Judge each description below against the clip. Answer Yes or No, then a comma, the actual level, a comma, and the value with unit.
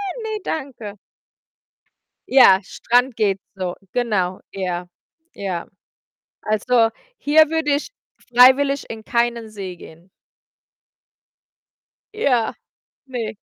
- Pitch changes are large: Yes, wide, 5.8 semitones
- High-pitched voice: Yes, high, 230 Hz